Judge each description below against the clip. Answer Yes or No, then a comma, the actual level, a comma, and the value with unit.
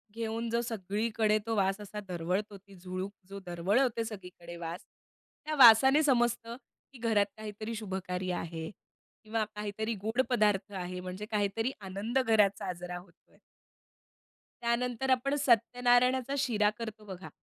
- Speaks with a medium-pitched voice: No, high, 215 Hz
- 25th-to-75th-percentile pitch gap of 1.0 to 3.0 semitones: No, average, 3.7 semitones